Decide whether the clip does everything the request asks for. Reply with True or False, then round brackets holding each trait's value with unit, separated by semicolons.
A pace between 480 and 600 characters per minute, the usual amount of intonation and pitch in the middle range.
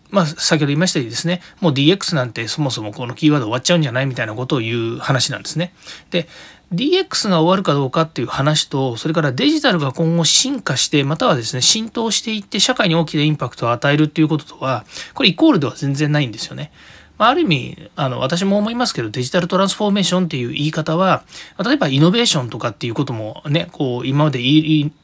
True (510 characters per minute; 4.8 semitones; 155 Hz)